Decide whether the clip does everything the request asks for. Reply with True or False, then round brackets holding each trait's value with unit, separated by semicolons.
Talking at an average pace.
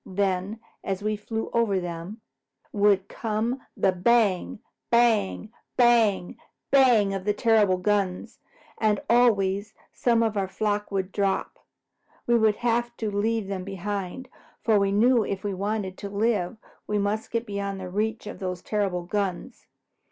True (145 wpm)